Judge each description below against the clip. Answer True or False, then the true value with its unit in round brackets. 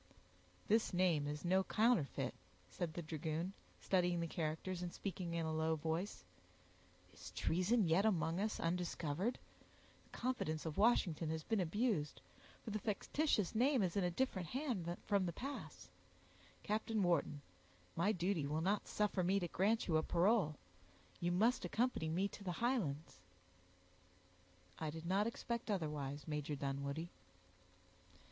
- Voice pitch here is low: False (175 Hz)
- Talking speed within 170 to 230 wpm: False (145 wpm)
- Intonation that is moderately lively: True (4.7 semitones)